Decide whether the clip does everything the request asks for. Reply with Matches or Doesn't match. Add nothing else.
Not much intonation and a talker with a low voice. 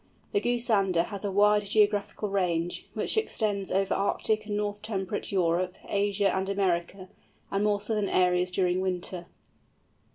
Doesn't match